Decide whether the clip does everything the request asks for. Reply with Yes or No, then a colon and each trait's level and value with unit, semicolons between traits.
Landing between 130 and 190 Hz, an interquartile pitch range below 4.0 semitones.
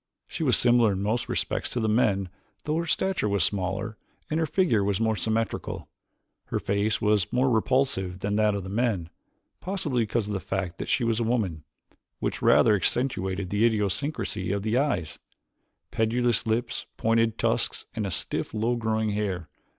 No: low, 110 Hz; average, 3.3 semitones